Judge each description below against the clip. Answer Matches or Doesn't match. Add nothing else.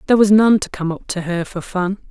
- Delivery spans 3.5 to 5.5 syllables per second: Doesn't match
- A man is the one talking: Doesn't match